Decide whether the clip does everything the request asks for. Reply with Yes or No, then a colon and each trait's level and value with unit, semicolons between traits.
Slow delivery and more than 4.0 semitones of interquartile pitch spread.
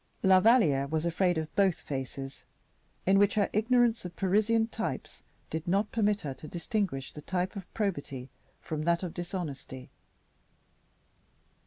No: average, 145 wpm; average, 5.0 semitones